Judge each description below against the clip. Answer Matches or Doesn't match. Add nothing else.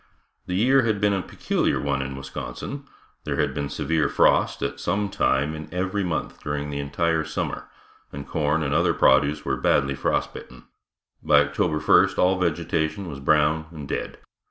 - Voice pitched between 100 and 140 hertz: Doesn't match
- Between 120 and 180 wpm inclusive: Matches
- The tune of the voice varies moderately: Matches